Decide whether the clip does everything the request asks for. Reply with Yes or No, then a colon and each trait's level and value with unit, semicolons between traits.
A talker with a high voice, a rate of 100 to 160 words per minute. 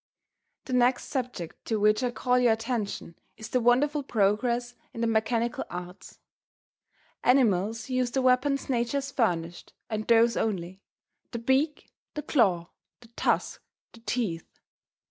Yes: high, 235 Hz; average, 140 wpm